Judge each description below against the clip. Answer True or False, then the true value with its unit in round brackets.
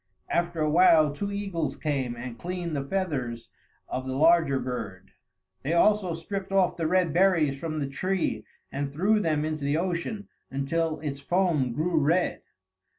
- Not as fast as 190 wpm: True (160 wpm)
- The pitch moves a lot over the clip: False (4.6 semitones)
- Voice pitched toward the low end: False (160 Hz)